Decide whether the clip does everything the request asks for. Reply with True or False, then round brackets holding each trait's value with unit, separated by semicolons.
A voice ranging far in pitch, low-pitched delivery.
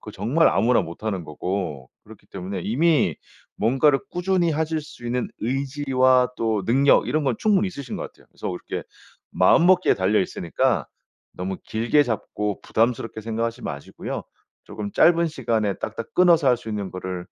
True (6.5 semitones; 115 Hz)